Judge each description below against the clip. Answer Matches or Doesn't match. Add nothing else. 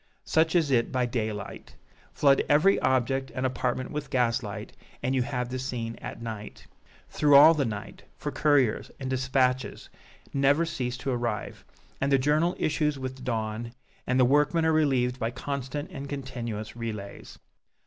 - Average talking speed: Matches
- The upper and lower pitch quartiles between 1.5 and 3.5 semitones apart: Matches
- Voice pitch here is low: Matches